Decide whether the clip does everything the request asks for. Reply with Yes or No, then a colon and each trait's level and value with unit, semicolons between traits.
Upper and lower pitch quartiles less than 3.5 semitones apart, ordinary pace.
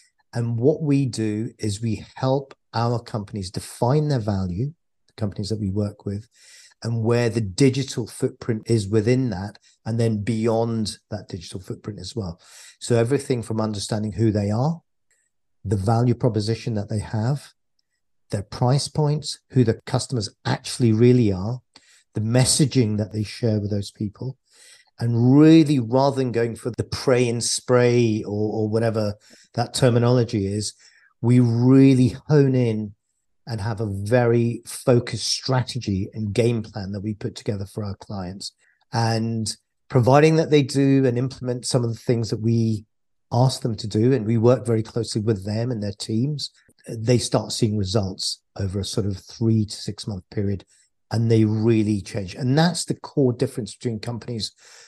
Yes: average, 2.8 semitones; average, 165 wpm